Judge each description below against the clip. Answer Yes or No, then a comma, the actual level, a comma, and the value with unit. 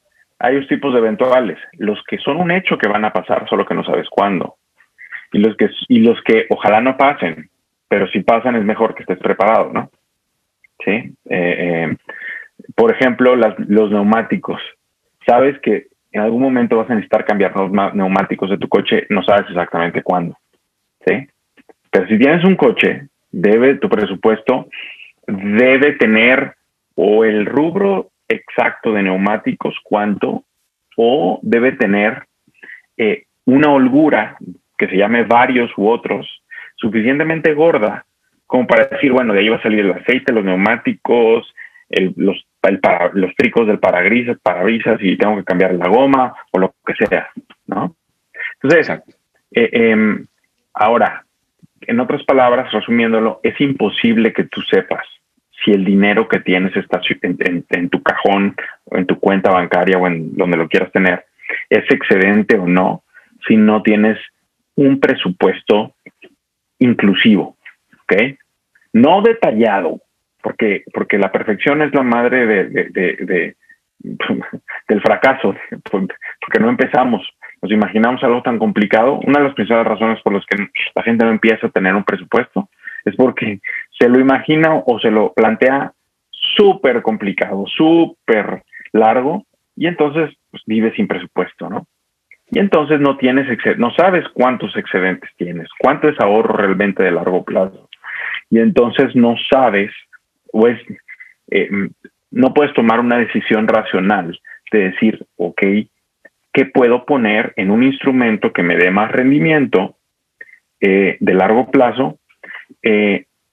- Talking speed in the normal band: Yes, average, 150 wpm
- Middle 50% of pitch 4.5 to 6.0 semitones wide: Yes, average, 5.2 semitones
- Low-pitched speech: Yes, low, 115 Hz